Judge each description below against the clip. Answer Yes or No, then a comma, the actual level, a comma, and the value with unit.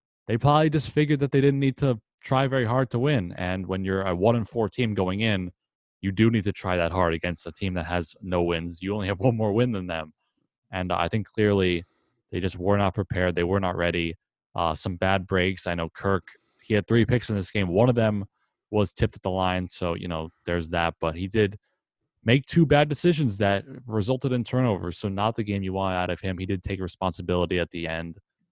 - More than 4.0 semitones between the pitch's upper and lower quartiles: Yes, average, 4.4 semitones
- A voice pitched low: Yes, very low, 95 Hz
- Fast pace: Yes, fast, 240 wpm